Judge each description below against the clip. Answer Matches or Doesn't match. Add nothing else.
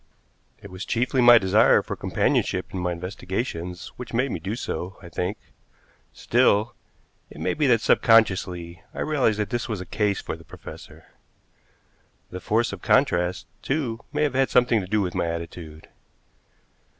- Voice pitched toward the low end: Matches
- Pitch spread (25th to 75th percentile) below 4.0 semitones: Doesn't match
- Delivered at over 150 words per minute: Matches